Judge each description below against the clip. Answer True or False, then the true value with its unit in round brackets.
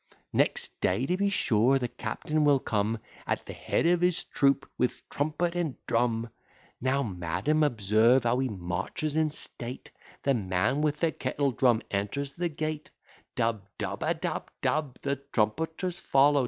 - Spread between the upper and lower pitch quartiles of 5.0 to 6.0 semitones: True (5.3 semitones)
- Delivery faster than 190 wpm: False (155 wpm)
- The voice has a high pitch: False (135 Hz)